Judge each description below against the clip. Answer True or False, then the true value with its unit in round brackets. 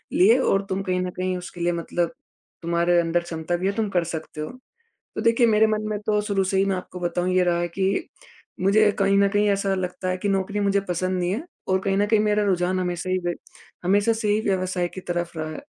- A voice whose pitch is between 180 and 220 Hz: True (185 Hz)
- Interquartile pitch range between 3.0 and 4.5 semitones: False (2.4 semitones)